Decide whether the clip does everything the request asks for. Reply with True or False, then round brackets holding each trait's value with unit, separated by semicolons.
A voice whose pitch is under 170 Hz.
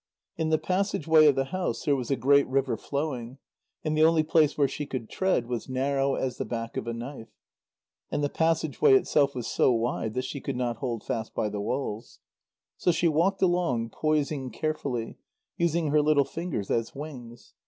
True (140 Hz)